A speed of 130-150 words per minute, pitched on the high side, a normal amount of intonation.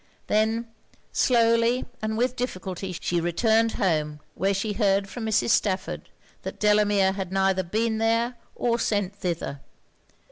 Yes: slow, 135 wpm; high, 210 Hz; average, 3.1 semitones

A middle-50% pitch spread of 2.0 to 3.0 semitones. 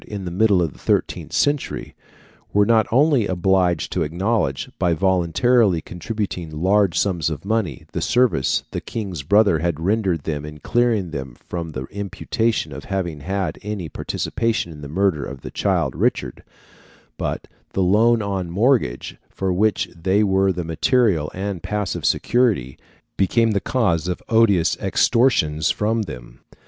No: average, 4.8 semitones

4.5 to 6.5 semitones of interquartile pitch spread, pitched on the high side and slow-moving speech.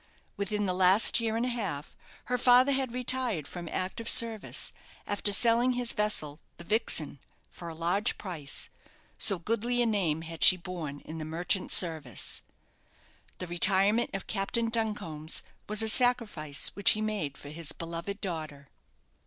No: wide, 5.6 semitones; high, 195 Hz; average, 155 wpm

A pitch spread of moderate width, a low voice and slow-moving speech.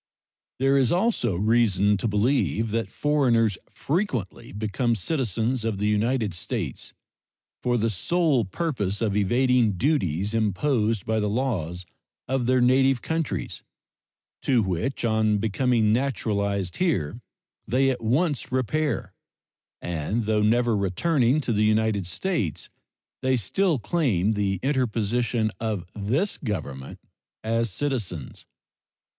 Yes: average, 4.3 semitones; low, 115 Hz; slow, 120 wpm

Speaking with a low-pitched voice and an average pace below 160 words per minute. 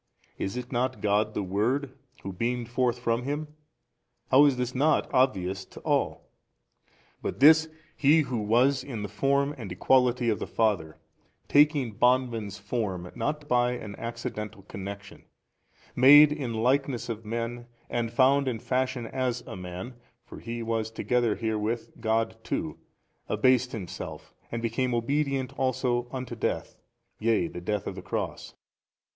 Yes: low, 120 Hz; average, 150 wpm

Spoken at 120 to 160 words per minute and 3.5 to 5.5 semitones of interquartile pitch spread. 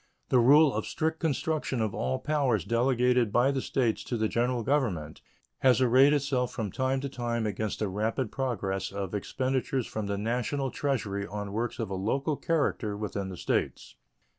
No: average, 175 wpm; average, 4.2 semitones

